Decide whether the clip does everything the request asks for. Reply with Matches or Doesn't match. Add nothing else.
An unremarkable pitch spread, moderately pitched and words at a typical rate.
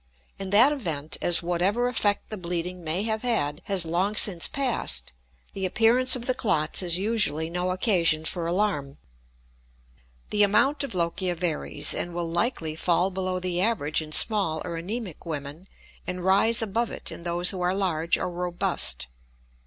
Matches